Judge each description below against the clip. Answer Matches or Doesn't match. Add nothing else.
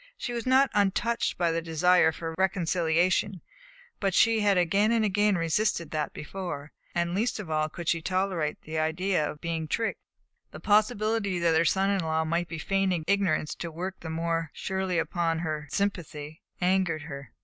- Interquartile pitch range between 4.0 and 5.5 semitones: Doesn't match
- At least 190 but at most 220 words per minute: Doesn't match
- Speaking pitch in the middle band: Matches